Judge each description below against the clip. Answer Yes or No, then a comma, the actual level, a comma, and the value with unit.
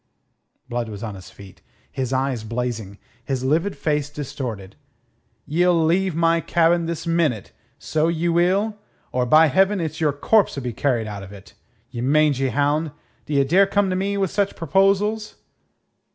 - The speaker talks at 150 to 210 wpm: Yes, average, 160 wpm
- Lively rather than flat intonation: Yes, wide, 5.8 semitones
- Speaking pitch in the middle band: Yes, medium, 155 Hz